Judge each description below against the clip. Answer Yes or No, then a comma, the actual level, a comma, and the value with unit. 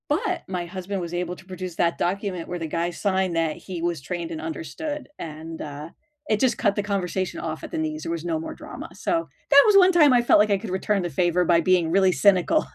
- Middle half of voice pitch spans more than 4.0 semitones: No, average, 3.4 semitones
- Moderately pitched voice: Yes, medium, 180 Hz